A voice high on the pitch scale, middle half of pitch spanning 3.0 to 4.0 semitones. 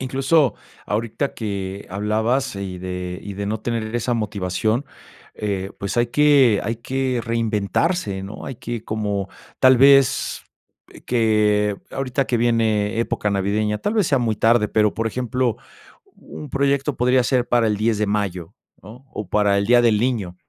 No: low, 110 Hz; average, 3.5 semitones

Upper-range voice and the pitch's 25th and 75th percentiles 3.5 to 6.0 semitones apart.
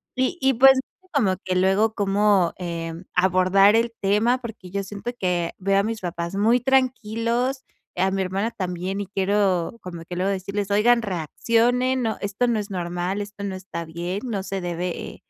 Yes: high, 200 Hz; average, 3.8 semitones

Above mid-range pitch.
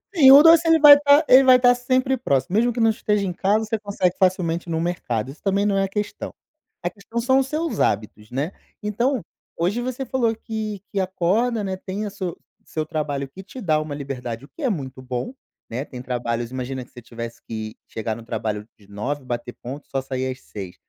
No: medium, 180 Hz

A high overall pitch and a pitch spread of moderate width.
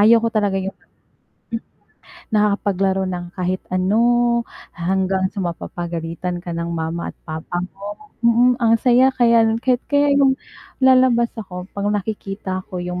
Yes: high, 195 Hz; average, 4.4 semitones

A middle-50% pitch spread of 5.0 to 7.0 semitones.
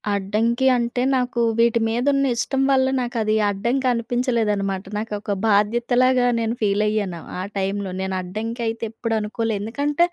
No: average, 2.9 semitones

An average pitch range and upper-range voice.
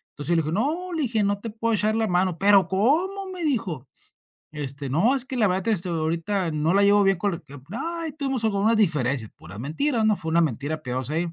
No: wide, 6.2 semitones; high, 195 Hz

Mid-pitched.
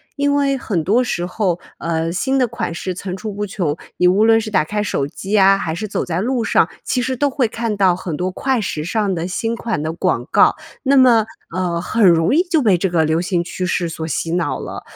No: high, 195 Hz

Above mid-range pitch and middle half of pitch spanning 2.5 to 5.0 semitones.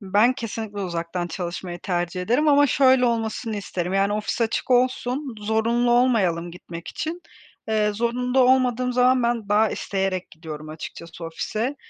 No: high, 220 Hz; wide, 5.4 semitones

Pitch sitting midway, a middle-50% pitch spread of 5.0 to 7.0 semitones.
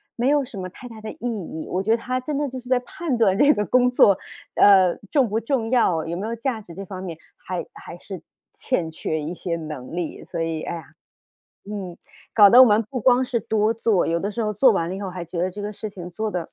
No: high, 205 Hz; average, 5.3 semitones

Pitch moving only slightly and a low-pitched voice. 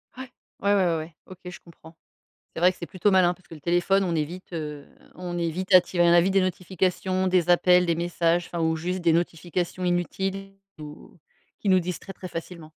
No: narrow, 1.8 semitones; medium, 175 Hz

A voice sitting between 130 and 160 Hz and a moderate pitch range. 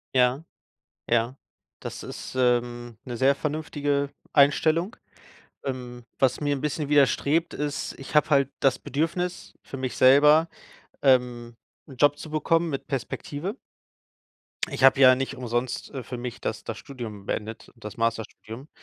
Yes: low, 135 Hz; average, 3.2 semitones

